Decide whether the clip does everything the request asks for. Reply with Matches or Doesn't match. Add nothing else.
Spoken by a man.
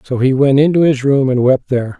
Matches